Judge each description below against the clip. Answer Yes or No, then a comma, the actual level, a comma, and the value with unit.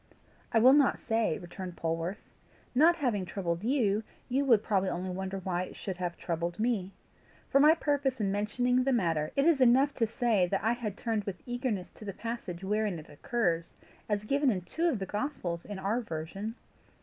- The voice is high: Yes, high, 210 Hz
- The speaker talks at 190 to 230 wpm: Yes, average, 195 wpm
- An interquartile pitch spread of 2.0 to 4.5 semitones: No, average, 5.3 semitones